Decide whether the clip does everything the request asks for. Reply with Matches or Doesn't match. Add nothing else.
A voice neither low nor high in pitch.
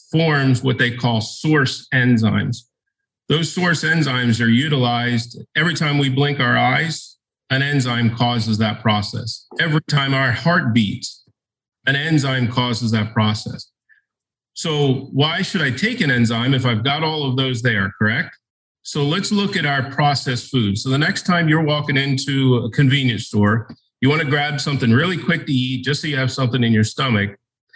Doesn't match